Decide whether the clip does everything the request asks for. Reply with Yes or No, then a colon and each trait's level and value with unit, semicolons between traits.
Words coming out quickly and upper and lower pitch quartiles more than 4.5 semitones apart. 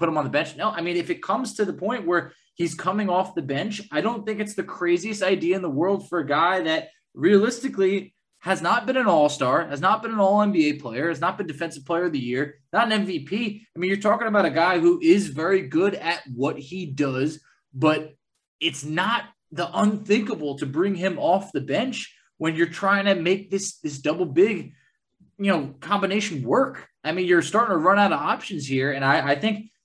Yes: fast, 225 wpm; average, 5.1 semitones